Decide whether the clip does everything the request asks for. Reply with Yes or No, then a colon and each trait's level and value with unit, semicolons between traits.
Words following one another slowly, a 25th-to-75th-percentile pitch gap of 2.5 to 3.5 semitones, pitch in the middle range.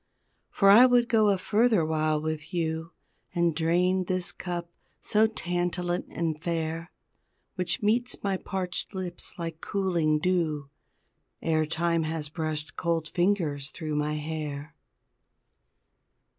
Yes: slow, 125 wpm; average, 2.9 semitones; medium, 170 Hz